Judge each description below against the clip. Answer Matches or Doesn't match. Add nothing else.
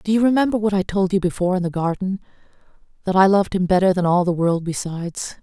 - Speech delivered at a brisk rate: Matches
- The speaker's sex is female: Matches